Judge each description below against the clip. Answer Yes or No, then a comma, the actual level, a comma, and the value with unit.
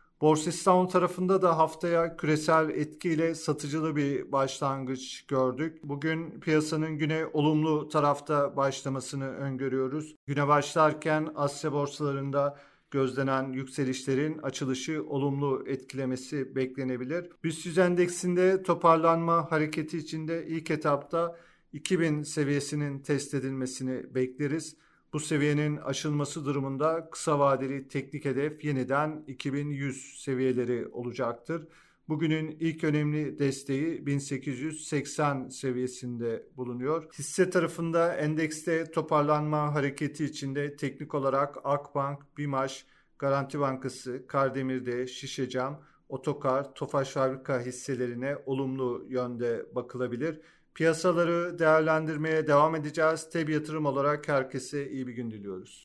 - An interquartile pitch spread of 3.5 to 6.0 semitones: No, average, 2.8 semitones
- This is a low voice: No, medium, 145 Hz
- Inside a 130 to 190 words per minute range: No, average, 100 wpm